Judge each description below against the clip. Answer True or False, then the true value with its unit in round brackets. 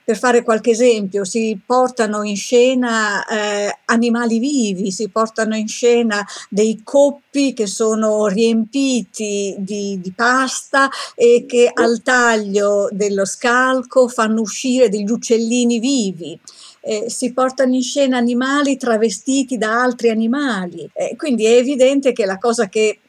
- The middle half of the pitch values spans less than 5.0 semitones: True (2.8 semitones)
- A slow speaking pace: False (135 wpm)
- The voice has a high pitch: True (235 Hz)